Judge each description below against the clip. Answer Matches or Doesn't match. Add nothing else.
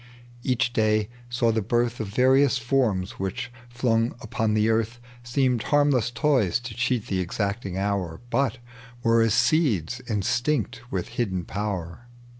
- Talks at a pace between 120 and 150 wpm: Matches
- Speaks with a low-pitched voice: Matches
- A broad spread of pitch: Doesn't match